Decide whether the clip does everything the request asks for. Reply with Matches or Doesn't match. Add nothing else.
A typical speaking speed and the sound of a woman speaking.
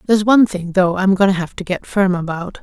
Doesn't match